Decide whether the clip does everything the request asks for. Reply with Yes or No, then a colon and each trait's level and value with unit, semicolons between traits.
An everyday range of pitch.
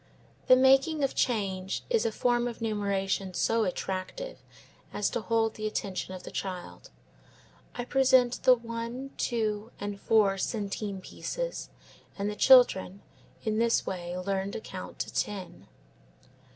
Yes: average, 3.8 semitones